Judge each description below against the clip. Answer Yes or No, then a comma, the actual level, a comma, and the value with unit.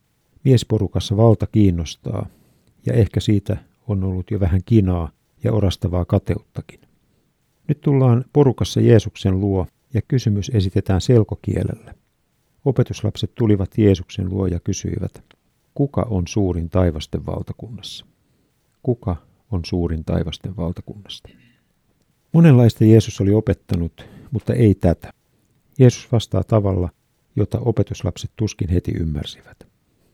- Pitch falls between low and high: No, low, 105 Hz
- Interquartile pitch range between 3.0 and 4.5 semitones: Yes, average, 3.8 semitones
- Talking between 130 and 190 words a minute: No, average, 110 wpm